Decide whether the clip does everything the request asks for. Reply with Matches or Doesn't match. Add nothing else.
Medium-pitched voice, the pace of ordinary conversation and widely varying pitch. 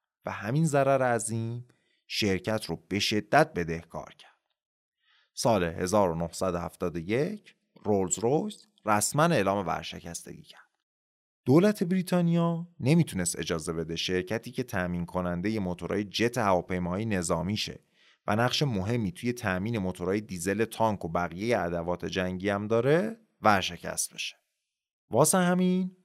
Doesn't match